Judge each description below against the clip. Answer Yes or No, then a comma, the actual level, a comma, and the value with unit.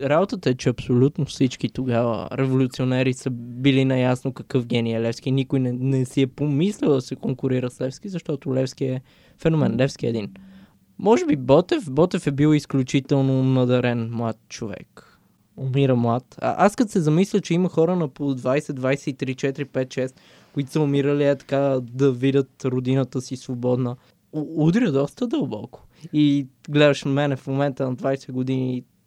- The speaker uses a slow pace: No, fast, 165 wpm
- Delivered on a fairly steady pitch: Yes, narrow, 2.0 semitones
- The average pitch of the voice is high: No, low, 135 Hz